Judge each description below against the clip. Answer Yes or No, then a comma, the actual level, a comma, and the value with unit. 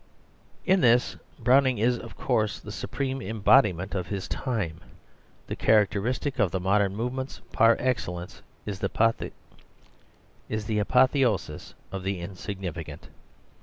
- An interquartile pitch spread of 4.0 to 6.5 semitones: Yes, average, 4.6 semitones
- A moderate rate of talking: No, slow, 115 wpm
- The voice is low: Yes, low, 110 Hz